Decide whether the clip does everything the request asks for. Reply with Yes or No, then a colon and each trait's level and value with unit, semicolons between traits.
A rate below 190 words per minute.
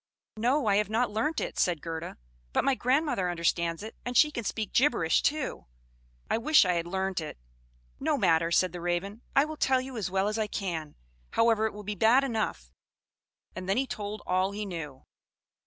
No: average, 200 wpm